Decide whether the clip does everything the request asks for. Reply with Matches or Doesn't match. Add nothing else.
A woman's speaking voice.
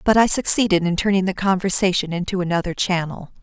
Matches